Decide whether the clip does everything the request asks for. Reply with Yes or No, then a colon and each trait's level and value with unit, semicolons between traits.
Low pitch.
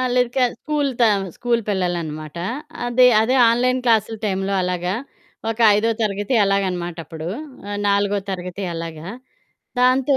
No: high, 200 Hz